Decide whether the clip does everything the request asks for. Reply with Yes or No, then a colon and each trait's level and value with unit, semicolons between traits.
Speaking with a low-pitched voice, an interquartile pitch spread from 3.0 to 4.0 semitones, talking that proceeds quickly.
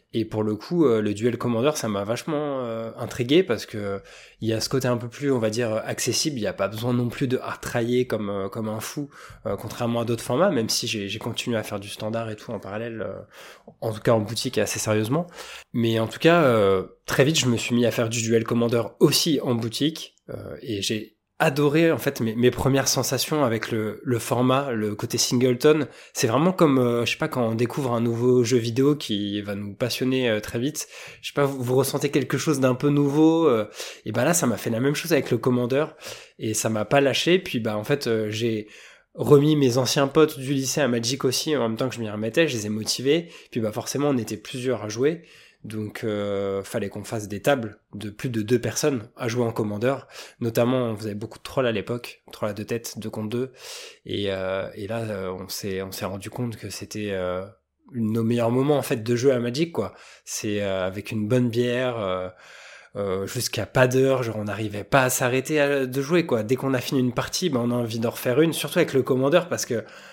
Yes: low, 120 Hz; average, 3.6 semitones; fast, 240 wpm